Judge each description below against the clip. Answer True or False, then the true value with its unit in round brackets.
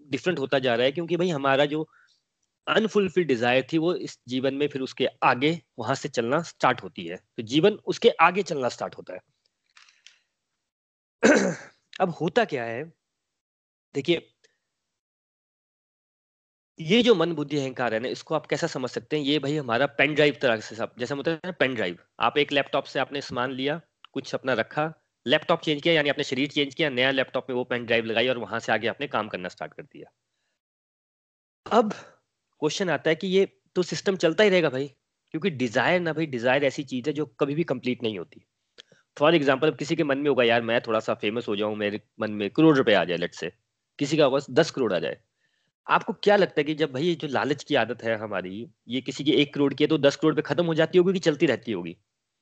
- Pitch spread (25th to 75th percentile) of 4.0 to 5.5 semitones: True (4.3 semitones)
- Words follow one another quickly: True (210 wpm)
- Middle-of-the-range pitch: True (145 Hz)